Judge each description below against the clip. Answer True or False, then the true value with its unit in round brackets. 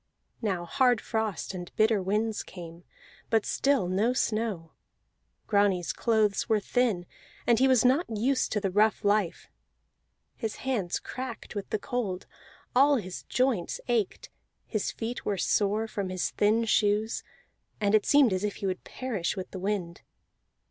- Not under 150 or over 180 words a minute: True (155 wpm)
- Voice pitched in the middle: False (215 Hz)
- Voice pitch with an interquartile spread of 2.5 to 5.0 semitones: True (3.5 semitones)